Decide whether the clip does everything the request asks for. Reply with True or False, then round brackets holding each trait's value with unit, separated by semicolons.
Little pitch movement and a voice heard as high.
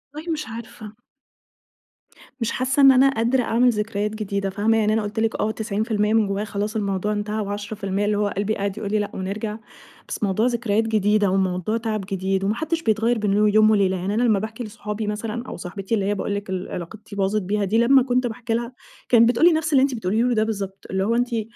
True (2.3 semitones; 215 Hz)